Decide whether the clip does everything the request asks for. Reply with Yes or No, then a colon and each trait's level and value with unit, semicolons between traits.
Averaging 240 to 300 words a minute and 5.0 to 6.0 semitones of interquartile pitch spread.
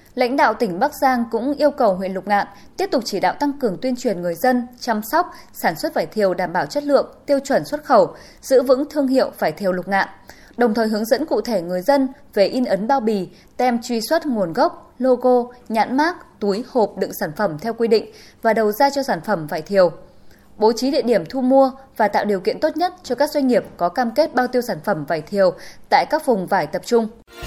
Yes: average, 245 wpm; wide, 5.5 semitones